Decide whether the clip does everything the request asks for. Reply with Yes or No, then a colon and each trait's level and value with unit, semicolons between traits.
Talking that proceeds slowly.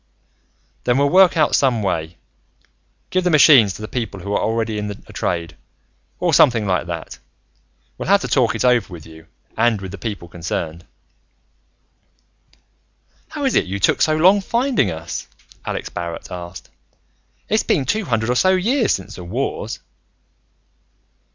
No: average, 160 wpm